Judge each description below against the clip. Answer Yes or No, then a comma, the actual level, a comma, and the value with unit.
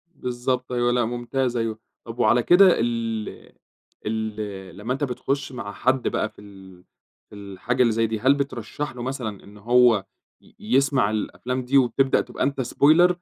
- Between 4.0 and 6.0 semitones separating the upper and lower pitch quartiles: No, average, 3.4 semitones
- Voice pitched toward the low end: Yes, low, 120 Hz